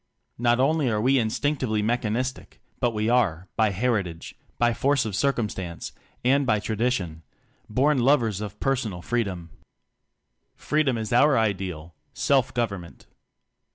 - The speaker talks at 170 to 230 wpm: No, slow, 135 wpm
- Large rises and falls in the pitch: No, average, 4.2 semitones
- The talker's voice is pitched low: Yes, low, 115 Hz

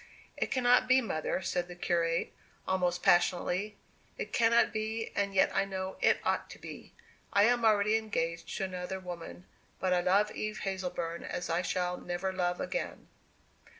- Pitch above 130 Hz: Yes, high, 190 Hz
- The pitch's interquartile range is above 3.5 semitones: No, average, 3.2 semitones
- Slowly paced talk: No, average, 165 wpm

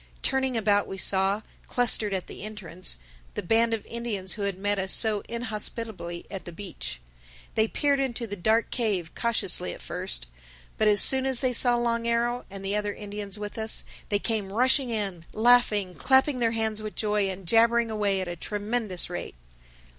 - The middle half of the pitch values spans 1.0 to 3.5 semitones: Yes, average, 3.1 semitones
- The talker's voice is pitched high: Yes, high, 215 Hz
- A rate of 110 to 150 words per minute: No, average, 185 wpm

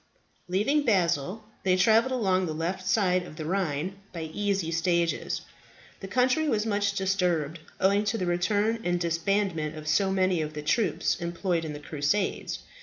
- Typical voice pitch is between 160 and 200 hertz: Yes, medium, 185 Hz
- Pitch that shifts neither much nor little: Yes, average, 3.6 semitones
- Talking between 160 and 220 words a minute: Yes, average, 165 wpm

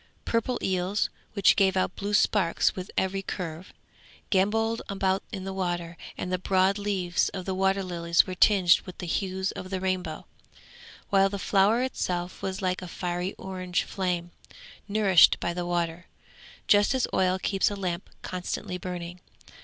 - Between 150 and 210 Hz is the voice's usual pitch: Yes, medium, 185 Hz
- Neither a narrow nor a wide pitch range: No, narrow, 1.6 semitones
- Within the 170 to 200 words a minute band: No, average, 160 wpm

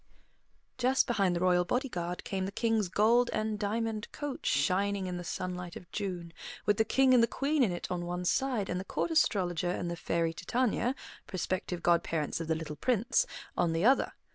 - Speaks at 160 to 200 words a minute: Yes, average, 195 wpm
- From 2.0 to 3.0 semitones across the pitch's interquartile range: No, average, 4.8 semitones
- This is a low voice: No, high, 190 Hz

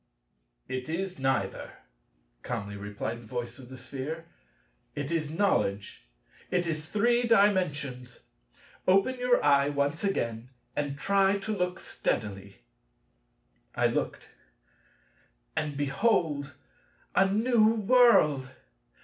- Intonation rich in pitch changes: Yes, wide, 7.2 semitones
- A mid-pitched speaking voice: Yes, medium, 150 Hz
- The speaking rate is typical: No, slow, 105 wpm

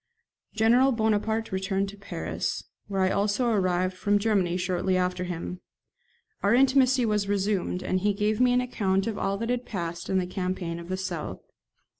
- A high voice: Yes, high, 200 Hz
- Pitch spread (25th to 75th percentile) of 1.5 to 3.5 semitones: Yes, average, 3.1 semitones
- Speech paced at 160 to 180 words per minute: Yes, average, 175 wpm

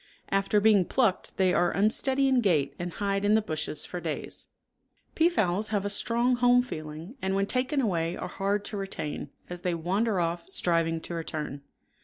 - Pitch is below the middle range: No, high, 195 Hz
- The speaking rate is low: No, average, 180 wpm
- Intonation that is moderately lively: Yes, average, 4.5 semitones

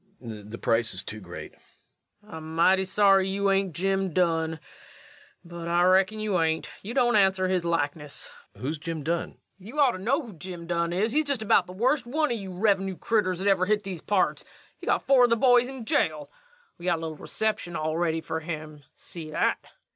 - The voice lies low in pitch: No, medium, 185 Hz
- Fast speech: Yes, fast, 215 wpm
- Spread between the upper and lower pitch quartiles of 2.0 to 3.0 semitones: No, average, 4.4 semitones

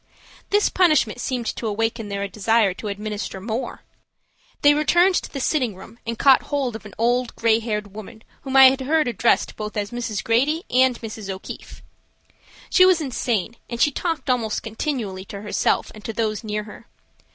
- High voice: Yes, high, 230 Hz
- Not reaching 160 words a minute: No, average, 180 wpm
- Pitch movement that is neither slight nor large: Yes, average, 3.8 semitones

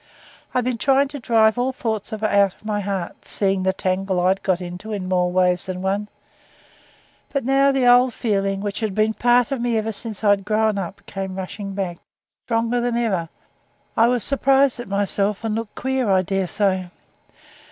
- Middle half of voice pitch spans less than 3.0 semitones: No, average, 3.8 semitones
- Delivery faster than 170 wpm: Yes, average, 195 wpm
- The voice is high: Yes, high, 210 Hz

